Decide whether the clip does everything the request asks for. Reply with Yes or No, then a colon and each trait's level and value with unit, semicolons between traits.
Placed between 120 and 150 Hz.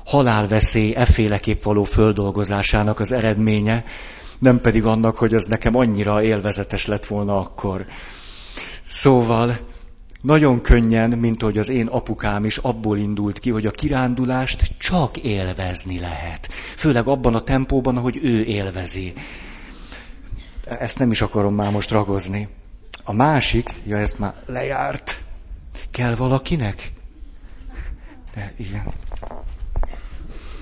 No: low, 105 Hz